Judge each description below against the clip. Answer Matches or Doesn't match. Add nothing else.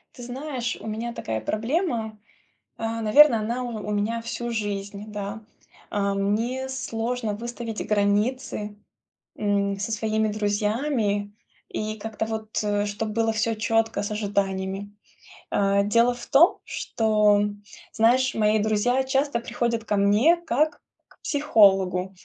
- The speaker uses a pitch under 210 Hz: Doesn't match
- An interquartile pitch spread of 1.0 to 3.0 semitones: Matches